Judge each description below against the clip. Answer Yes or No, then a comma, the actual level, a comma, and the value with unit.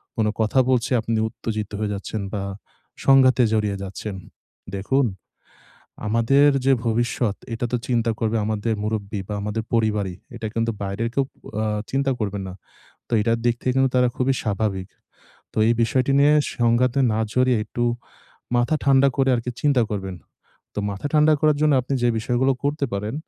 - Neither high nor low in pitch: No, low, 115 Hz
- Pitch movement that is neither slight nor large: Yes, average, 3.6 semitones